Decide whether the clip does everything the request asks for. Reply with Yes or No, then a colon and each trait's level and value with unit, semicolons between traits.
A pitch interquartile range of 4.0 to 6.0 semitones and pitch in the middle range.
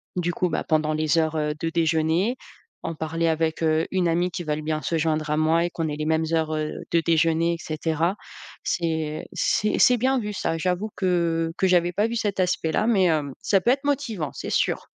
No: narrow, 2.5 semitones; medium, 165 Hz